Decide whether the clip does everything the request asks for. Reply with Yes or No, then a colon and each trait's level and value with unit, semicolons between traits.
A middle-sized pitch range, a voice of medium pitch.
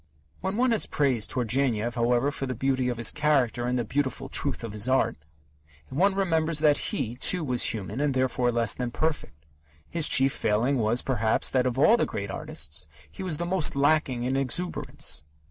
No: average, 4.2 semitones; low, 130 Hz